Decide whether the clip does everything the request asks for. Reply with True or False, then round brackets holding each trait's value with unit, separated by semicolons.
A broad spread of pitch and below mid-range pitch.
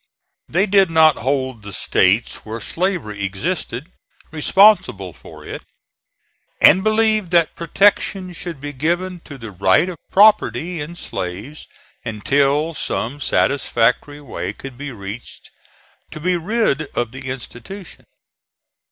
False (7.0 semitones; 145 Hz)